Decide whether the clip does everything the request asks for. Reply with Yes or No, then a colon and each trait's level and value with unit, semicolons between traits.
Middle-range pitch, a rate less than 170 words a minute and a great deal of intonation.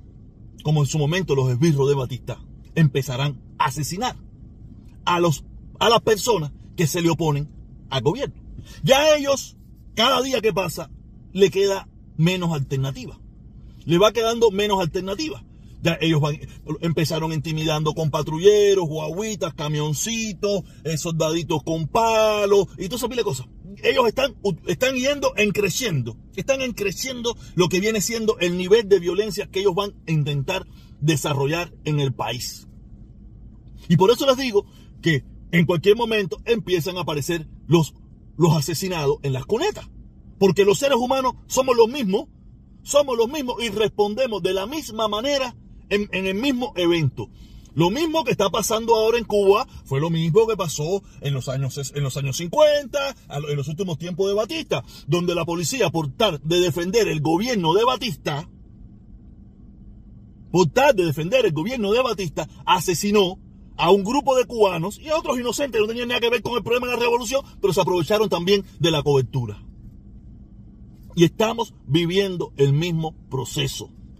Yes: medium, 180 Hz; average, 160 wpm; wide, 6.7 semitones